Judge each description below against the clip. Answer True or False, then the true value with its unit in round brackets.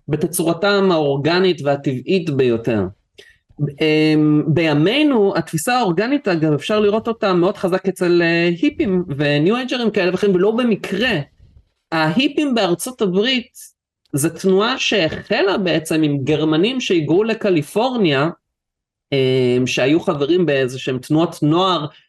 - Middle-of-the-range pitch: True (175 Hz)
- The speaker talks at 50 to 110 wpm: True (105 wpm)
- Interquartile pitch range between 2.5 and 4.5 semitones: False (5.2 semitones)